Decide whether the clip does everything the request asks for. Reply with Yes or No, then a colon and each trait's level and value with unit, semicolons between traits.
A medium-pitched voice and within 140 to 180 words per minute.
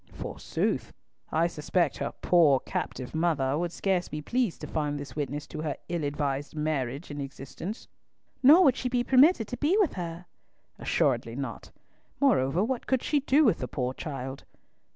Yes: medium, 165 Hz; average, 170 wpm